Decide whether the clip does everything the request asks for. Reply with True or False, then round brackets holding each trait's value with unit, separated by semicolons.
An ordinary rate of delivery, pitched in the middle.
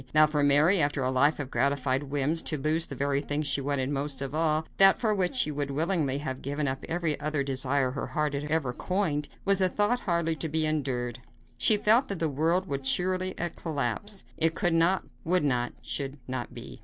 False (210 wpm; 150 Hz)